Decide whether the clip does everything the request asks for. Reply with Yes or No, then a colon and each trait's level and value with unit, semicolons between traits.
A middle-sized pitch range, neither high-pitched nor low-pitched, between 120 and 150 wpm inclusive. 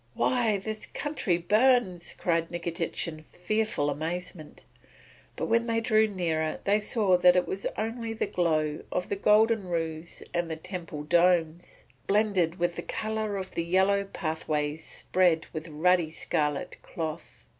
Yes: average, 4.3 semitones; medium, 180 Hz; average, 145 wpm